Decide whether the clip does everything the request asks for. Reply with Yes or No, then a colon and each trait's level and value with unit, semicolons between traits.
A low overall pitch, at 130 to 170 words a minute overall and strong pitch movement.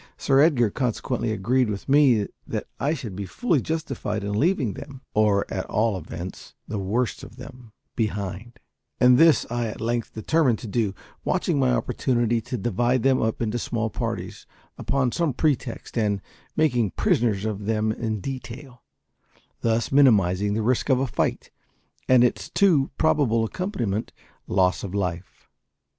No: low, 115 Hz; average, 155 wpm; average, 4.0 semitones